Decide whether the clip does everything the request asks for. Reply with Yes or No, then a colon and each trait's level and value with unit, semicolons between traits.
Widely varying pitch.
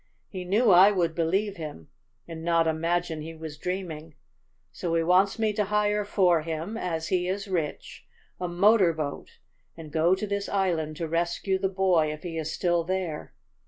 No: average, 3.0 semitones